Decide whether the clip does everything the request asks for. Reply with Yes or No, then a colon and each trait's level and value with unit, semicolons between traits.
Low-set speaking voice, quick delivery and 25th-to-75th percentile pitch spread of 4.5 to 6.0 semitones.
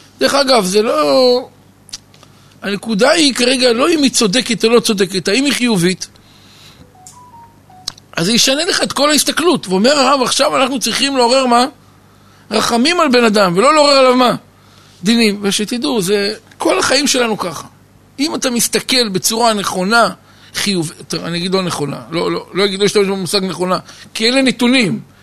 No: high, 230 Hz; fast, 160 wpm; average, 5.1 semitones